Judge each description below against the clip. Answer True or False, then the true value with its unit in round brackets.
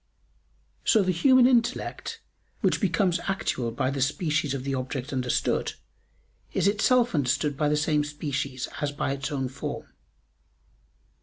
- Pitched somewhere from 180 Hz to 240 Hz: False (150 Hz)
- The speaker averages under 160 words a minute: True (140 wpm)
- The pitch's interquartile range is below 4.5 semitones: False (5.6 semitones)